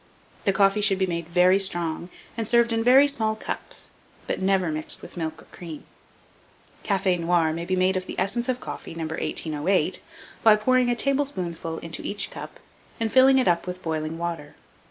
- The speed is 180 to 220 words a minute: Yes, average, 185 wpm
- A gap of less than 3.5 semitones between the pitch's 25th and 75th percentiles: No, average, 4.8 semitones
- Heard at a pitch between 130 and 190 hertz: Yes, medium, 185 Hz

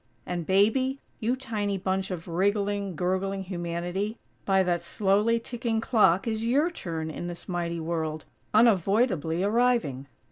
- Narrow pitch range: No, average, 4.4 semitones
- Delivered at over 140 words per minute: No, slow, 135 wpm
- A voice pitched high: Yes, high, 195 Hz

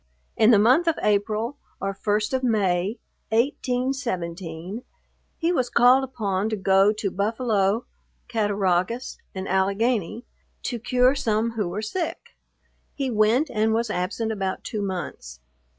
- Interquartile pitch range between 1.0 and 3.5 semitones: No, average, 3.9 semitones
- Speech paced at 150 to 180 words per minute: No, slow, 135 wpm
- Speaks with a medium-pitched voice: No, high, 215 Hz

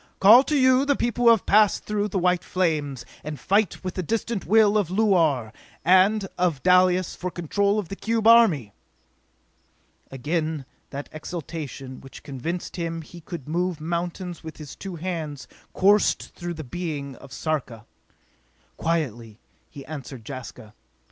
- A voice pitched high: No, medium, 170 Hz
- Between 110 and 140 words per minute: No, average, 150 wpm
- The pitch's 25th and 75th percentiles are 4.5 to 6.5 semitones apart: Yes, average, 5.2 semitones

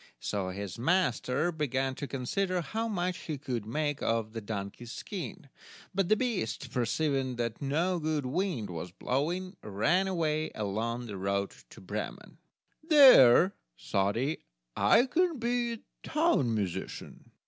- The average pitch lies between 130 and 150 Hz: Yes, medium, 140 Hz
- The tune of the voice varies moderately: No, wide, 8.3 semitones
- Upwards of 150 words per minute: No, slow, 135 wpm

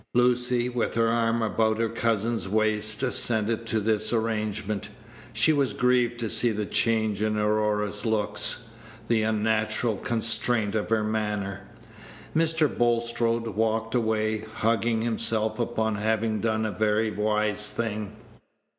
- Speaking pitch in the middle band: No, low, 110 Hz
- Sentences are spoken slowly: Yes, slow, 130 wpm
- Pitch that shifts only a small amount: Yes, narrow, 1.4 semitones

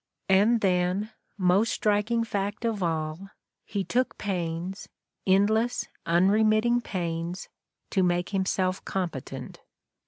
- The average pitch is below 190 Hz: No, high, 195 Hz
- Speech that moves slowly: Yes, slow, 100 wpm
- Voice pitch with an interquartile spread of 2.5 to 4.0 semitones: Yes, average, 3.3 semitones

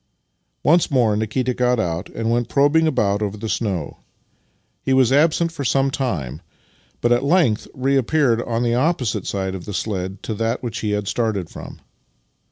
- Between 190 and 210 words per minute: No, average, 175 wpm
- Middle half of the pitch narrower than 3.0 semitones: No, average, 4.5 semitones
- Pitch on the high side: No, low, 120 Hz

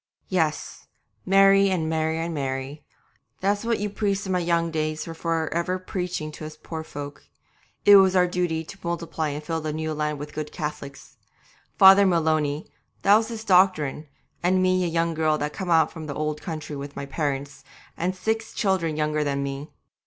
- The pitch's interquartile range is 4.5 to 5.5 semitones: No, average, 3.4 semitones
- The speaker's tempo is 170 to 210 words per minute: Yes, average, 190 wpm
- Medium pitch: Yes, medium, 160 Hz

